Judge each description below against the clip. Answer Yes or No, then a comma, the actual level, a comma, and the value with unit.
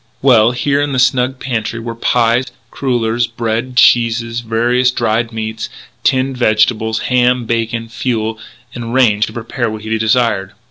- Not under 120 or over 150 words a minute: Yes, average, 145 wpm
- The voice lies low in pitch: Yes, low, 115 Hz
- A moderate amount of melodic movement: No, narrow, 1.9 semitones